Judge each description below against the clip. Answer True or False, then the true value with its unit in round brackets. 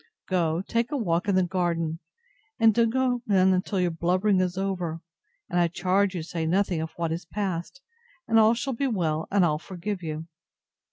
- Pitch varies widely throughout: False (3.5 semitones)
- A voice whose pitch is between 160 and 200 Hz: True (185 Hz)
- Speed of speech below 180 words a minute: False (190 wpm)